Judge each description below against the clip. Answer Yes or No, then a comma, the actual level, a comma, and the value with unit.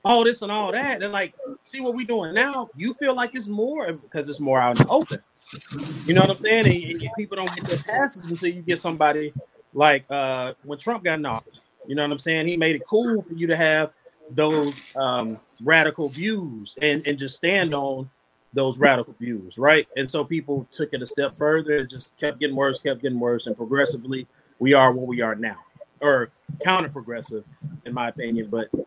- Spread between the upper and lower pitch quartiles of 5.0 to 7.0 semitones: Yes, average, 5.3 semitones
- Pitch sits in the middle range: Yes, medium, 150 Hz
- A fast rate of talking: Yes, fast, 215 wpm